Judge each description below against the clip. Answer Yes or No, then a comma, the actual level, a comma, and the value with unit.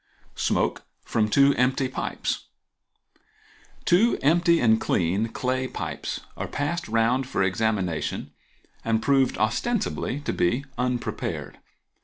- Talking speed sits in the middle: No, slow, 105 wpm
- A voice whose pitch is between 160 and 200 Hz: No, low, 125 Hz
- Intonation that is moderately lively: Yes, average, 4.1 semitones